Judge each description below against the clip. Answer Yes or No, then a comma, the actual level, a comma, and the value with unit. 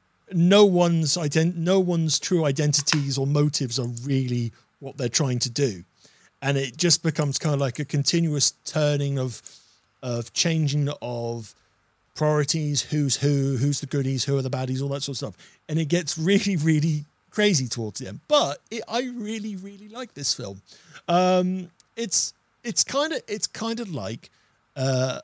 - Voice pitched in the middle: Yes, medium, 145 Hz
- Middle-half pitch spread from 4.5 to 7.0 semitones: Yes, average, 4.9 semitones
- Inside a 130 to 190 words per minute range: Yes, average, 170 wpm